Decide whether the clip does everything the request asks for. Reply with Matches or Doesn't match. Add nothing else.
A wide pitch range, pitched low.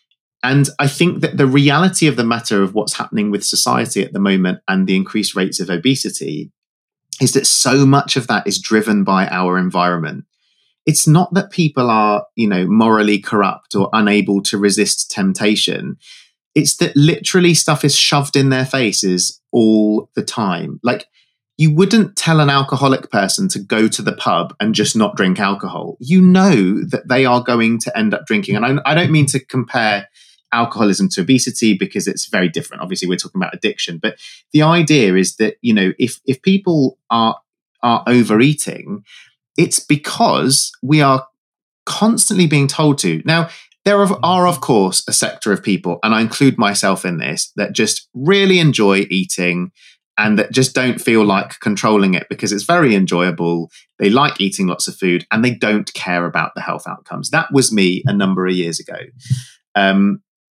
Matches